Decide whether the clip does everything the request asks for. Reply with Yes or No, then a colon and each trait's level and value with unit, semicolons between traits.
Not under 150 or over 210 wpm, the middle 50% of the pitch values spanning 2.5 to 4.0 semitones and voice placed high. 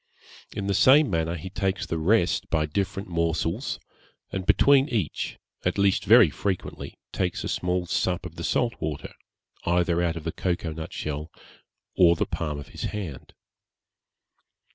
No: average, 160 wpm; average, 3.3 semitones; very low, 90 Hz